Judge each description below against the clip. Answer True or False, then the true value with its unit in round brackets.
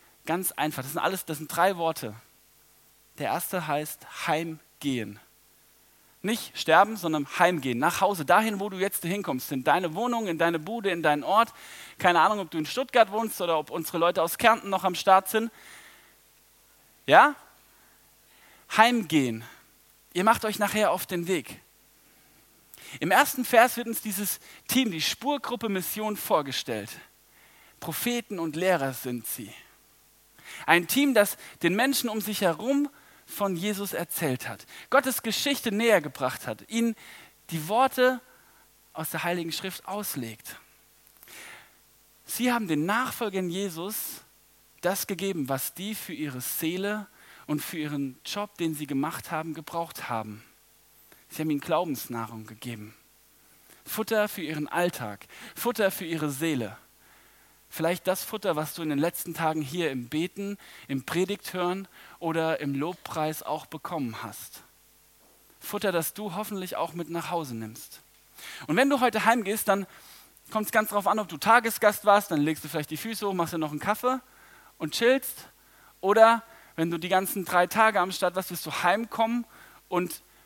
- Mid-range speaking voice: True (180 Hz)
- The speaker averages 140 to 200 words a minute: True (155 wpm)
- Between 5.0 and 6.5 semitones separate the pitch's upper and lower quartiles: True (5.5 semitones)